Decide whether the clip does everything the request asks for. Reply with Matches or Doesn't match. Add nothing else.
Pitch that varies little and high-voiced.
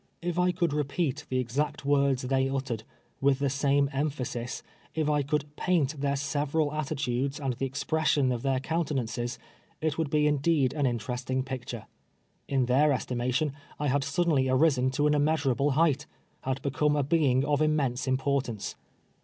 Doesn't match